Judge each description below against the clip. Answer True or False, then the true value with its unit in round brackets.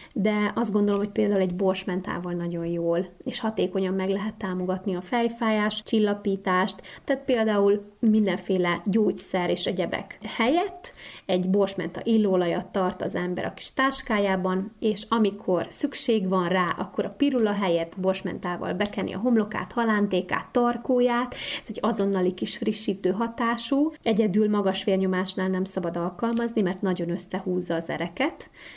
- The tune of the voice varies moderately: True (3.2 semitones)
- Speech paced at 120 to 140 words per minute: True (135 wpm)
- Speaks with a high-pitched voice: True (200 Hz)